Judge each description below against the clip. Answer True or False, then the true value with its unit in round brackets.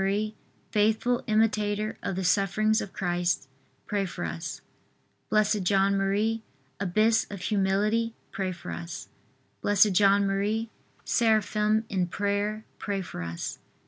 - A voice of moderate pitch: False (205 Hz)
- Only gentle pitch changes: True (2.0 semitones)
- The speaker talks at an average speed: False (120 wpm)